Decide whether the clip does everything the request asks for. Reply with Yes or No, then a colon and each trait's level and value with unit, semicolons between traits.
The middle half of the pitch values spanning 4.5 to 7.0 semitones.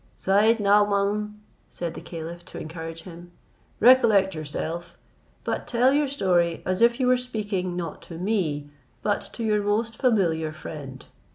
Yes: average, 4.8 semitones